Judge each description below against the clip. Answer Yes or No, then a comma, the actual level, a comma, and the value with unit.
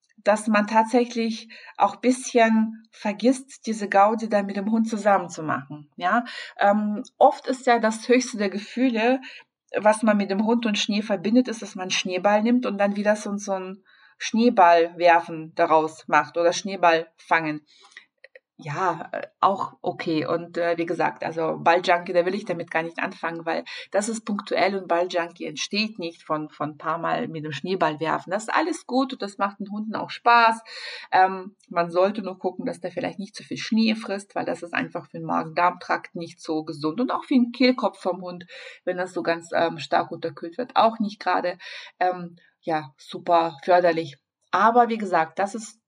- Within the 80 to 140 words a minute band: No, fast, 190 wpm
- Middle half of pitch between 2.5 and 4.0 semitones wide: No, average, 4.8 semitones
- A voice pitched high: Yes, high, 195 Hz